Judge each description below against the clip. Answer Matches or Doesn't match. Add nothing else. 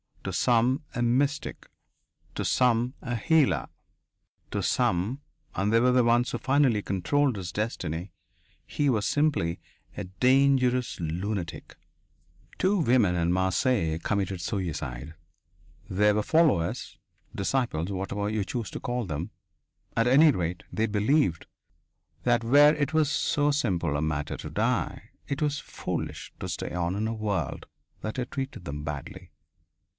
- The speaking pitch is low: Matches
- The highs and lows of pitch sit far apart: Matches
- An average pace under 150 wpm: Matches